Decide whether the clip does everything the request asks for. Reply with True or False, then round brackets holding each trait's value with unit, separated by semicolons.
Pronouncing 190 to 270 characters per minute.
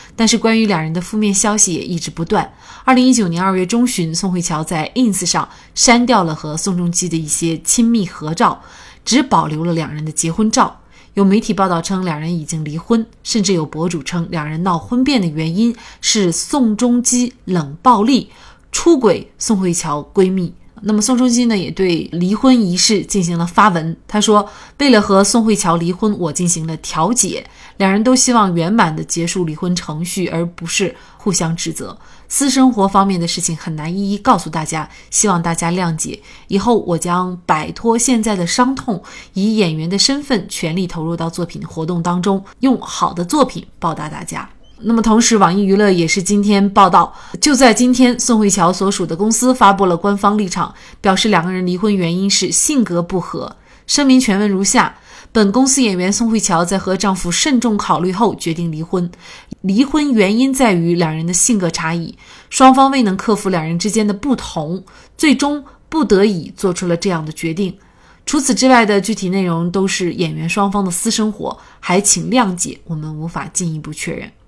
False (285 characters per minute)